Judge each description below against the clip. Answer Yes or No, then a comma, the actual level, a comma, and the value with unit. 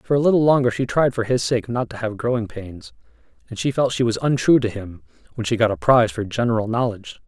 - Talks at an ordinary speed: No, fast, 245 wpm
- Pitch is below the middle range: Yes, low, 115 Hz